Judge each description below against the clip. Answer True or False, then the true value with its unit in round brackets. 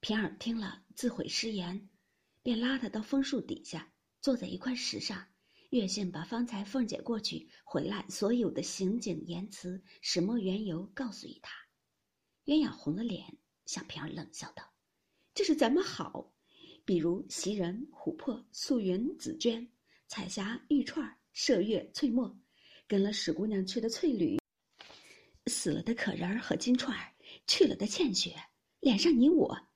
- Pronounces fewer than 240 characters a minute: True (225 characters per minute)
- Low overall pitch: False (230 Hz)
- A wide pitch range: True (5.7 semitones)